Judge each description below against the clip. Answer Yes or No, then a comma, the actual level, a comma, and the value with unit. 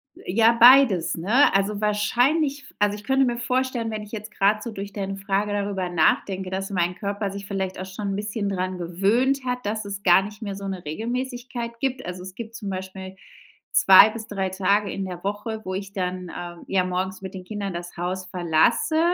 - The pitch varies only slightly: No, average, 3.2 semitones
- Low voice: No, high, 200 Hz